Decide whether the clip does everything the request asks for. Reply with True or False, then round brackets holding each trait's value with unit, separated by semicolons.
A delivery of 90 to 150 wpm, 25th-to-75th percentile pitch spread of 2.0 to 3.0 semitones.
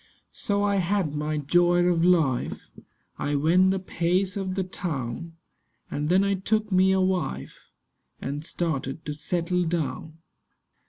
False (145 wpm; 3.8 semitones)